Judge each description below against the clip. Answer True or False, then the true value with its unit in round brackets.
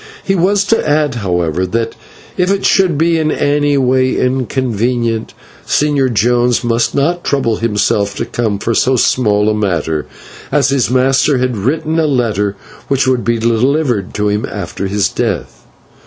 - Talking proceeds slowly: False (165 wpm)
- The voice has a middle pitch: False (125 Hz)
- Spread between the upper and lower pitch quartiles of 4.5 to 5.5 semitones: True (5.1 semitones)